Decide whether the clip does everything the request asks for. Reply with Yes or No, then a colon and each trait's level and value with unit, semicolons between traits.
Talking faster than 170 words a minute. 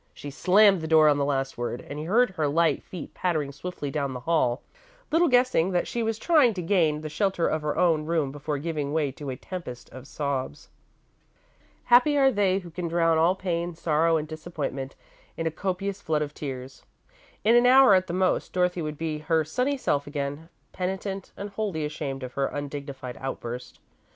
Yes: average, 195 wpm